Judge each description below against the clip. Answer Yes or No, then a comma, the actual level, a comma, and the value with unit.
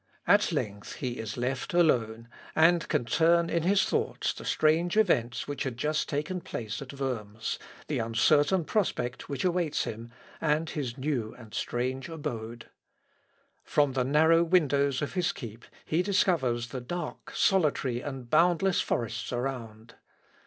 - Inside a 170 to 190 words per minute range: No, average, 145 wpm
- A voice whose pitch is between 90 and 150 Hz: Yes, medium, 140 Hz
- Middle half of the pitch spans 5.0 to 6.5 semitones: Yes, wide, 5.5 semitones